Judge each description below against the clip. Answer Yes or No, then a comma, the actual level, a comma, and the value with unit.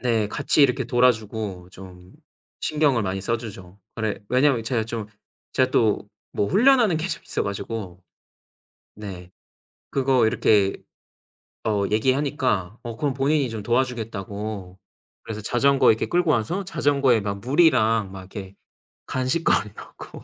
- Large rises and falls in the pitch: No, average, 4.7 semitones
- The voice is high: No, low, 115 Hz